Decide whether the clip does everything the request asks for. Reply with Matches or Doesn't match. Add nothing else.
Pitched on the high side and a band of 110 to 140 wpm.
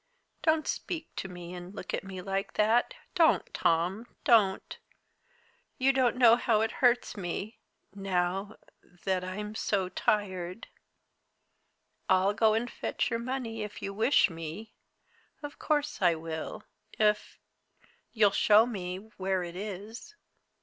Matches